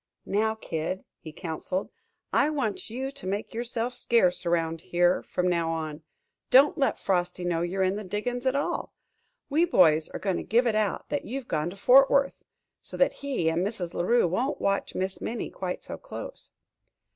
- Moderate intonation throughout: No, wide, 5.8 semitones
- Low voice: No, high, 195 Hz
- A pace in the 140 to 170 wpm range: No, average, 190 wpm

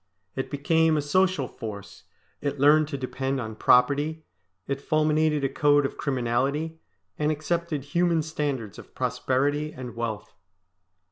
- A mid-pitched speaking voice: Yes, medium, 145 Hz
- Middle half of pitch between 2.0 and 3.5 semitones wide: Yes, average, 2.9 semitones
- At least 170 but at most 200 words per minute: No, slow, 135 wpm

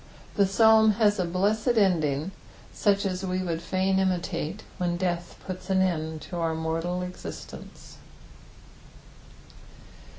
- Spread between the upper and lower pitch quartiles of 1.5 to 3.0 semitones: Yes, narrow, 2.5 semitones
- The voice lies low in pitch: No, medium, 185 Hz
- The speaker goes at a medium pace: No, slow, 125 wpm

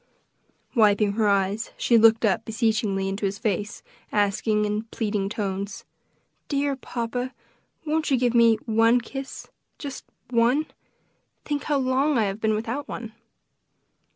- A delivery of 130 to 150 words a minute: Yes, slow, 135 wpm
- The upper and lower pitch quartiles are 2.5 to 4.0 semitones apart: Yes, average, 3.4 semitones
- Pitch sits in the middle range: No, high, 225 Hz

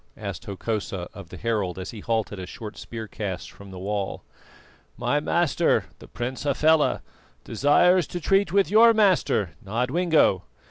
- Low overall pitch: Yes, low, 115 Hz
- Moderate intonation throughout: No, wide, 8.6 semitones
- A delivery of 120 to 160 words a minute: Yes, average, 150 wpm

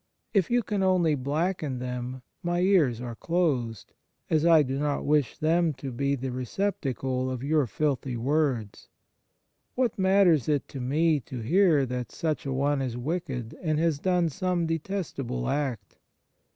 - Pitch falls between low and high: Yes, medium, 145 Hz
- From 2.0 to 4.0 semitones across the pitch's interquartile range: No, average, 4.9 semitones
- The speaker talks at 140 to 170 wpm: Yes, average, 155 wpm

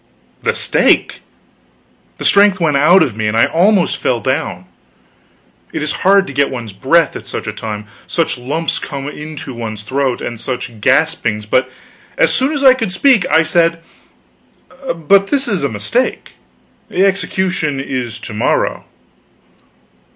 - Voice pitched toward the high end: No, medium, 150 Hz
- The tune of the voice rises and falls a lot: Yes, wide, 7.5 semitones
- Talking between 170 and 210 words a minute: No, average, 155 wpm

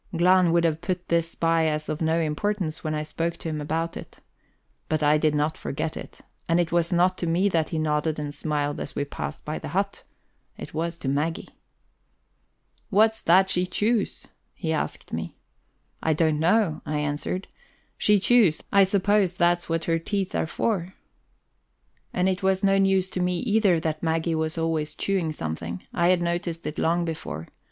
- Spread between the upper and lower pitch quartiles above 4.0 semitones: No, average, 2.9 semitones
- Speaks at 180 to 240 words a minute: Yes, average, 185 wpm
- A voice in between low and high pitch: Yes, medium, 165 Hz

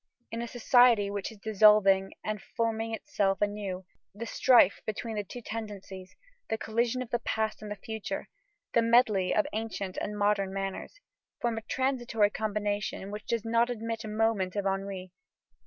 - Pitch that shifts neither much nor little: No, narrow, 2.3 semitones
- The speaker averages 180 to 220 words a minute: No, average, 165 wpm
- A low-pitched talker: No, high, 215 Hz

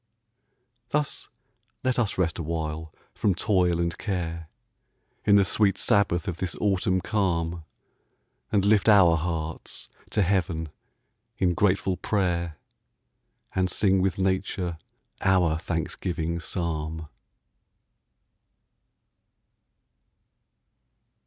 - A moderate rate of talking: No, slow, 95 wpm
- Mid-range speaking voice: No, very low, 90 Hz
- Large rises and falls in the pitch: No, average, 2.7 semitones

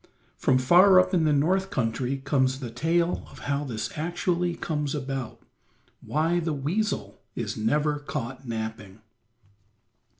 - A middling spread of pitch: Yes, average, 4.8 semitones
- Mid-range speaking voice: Yes, medium, 145 Hz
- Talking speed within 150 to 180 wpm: No, slow, 135 wpm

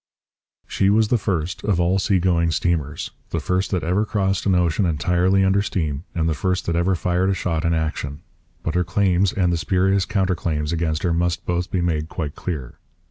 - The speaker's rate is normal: No, fast, 210 wpm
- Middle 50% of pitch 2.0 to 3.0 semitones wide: Yes, narrow, 2.5 semitones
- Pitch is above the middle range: No, very low, 90 Hz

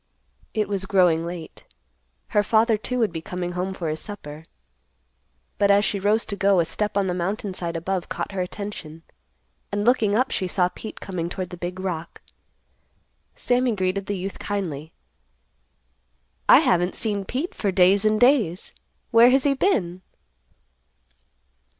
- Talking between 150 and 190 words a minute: Yes, average, 160 wpm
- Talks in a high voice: Yes, high, 195 Hz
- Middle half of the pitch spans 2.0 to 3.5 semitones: Yes, average, 3.1 semitones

